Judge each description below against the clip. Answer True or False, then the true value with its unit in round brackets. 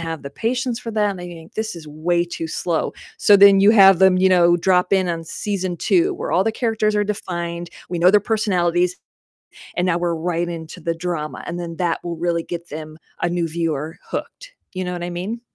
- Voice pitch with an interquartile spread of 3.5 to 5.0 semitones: False (2.8 semitones)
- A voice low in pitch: False (175 Hz)